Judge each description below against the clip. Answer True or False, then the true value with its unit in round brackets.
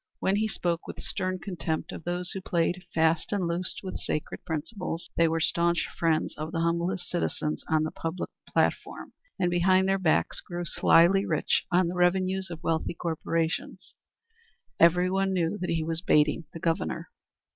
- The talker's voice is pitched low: False (175 Hz)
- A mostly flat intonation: True (2.1 semitones)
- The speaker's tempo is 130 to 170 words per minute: True (165 wpm)